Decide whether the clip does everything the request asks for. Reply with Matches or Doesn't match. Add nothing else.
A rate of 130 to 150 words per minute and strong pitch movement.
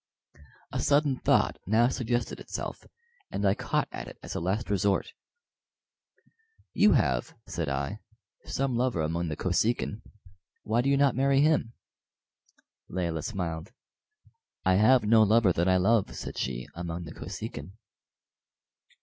Matches